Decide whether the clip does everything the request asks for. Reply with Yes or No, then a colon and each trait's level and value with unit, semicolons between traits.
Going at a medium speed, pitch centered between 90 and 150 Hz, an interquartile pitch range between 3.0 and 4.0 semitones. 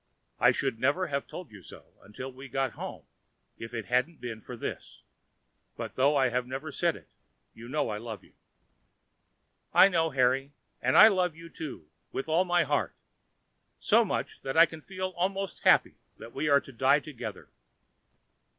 No: average, 180 wpm; medium, 140 Hz; average, 4.9 semitones